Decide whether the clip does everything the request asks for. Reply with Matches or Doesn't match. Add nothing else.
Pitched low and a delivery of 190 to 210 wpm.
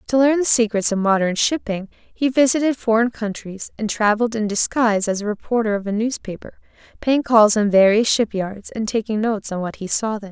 Doesn't match